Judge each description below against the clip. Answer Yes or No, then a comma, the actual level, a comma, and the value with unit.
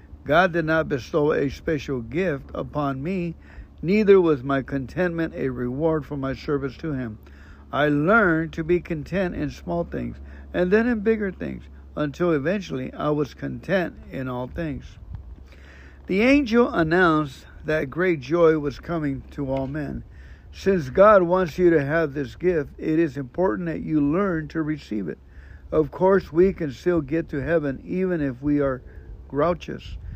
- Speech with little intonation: No, average, 5.1 semitones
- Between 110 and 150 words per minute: No, average, 165 wpm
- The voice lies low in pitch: No, medium, 150 Hz